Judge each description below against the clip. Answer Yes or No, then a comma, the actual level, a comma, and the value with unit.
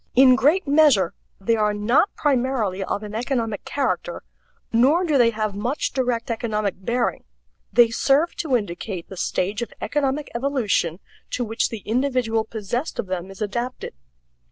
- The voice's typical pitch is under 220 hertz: No, high, 235 Hz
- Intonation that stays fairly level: No, average, 4.3 semitones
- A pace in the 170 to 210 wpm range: No, average, 155 wpm